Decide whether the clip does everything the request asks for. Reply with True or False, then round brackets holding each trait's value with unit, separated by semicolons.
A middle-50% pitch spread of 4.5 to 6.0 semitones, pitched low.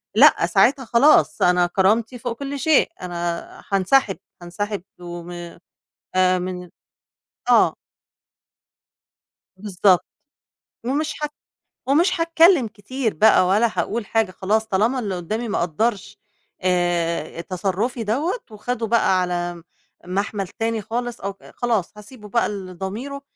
False (4.8 semitones; 210 Hz)